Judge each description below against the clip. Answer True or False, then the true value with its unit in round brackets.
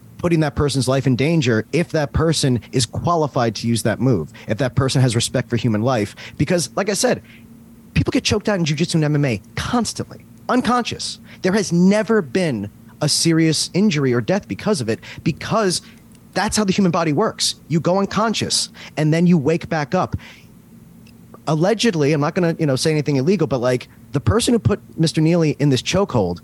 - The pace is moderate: True (195 wpm)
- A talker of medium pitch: True (150 Hz)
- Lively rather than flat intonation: True (6.4 semitones)